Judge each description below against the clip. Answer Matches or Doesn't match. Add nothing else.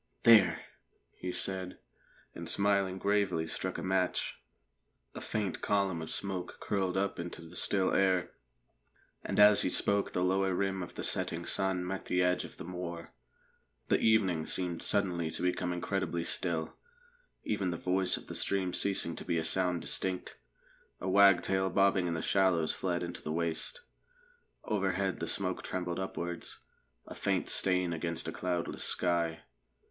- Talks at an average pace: Matches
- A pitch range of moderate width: Doesn't match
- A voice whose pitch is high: Doesn't match